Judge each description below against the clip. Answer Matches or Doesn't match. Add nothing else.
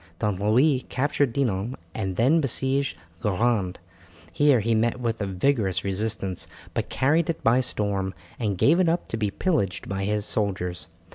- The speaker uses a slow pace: Doesn't match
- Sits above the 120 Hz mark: Doesn't match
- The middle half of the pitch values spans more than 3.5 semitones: Matches